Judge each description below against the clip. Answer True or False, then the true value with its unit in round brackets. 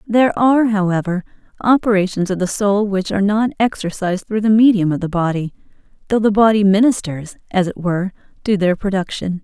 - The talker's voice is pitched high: True (200 Hz)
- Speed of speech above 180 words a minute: False (170 wpm)